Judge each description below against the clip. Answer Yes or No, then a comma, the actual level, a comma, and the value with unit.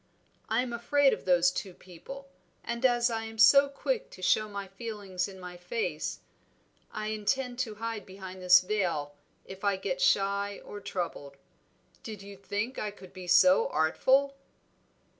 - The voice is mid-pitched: No, high, 200 Hz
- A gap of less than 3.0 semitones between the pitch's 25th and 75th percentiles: No, average, 3.9 semitones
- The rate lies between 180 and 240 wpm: No, average, 160 wpm